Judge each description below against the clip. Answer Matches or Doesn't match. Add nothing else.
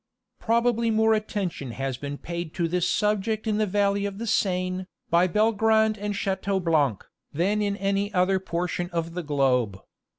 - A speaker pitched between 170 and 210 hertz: Matches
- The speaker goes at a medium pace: Matches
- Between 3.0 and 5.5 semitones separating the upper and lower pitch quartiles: Matches